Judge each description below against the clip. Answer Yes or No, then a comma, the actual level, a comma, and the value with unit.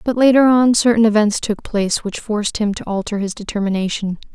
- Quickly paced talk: No, average, 195 wpm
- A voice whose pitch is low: No, high, 215 Hz